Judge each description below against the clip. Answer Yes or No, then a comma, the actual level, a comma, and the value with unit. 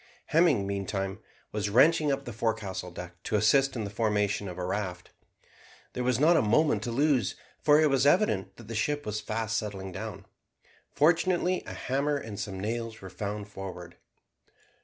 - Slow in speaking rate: No, average, 175 wpm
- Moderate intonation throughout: No, wide, 5.9 semitones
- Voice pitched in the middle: No, low, 110 Hz